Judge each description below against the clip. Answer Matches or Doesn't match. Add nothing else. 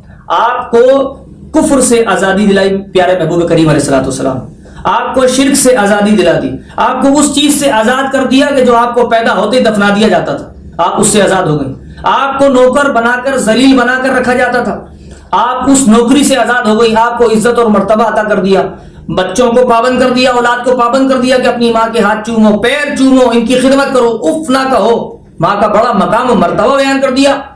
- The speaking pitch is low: Doesn't match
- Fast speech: Matches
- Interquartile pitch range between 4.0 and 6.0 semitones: Doesn't match